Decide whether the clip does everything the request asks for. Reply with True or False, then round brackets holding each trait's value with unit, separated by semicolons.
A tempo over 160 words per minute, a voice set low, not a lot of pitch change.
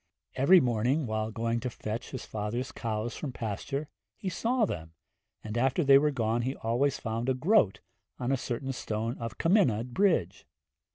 False (170 wpm; 120 Hz; 3.8 semitones)